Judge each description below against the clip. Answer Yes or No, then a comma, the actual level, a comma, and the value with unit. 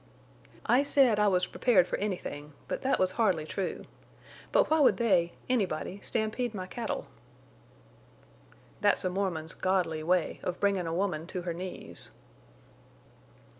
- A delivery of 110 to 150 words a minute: Yes, slow, 135 wpm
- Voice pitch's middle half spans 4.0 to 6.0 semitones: No, average, 3.6 semitones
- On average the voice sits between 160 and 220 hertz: Yes, high, 190 Hz